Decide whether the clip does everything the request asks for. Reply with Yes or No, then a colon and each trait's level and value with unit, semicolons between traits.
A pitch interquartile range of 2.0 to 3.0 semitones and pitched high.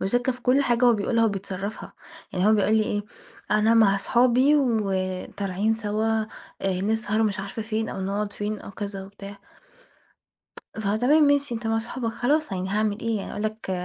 Yes: average, 2.7 semitones; high, 215 Hz